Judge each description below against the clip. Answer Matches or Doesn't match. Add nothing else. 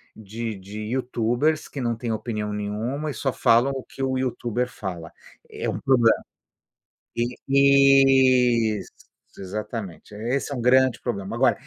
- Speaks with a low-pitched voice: Matches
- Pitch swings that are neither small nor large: Matches